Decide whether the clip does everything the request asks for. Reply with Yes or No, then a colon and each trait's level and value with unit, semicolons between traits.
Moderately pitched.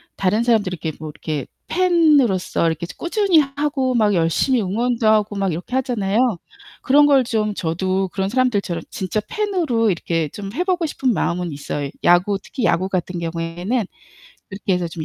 No: high, 205 Hz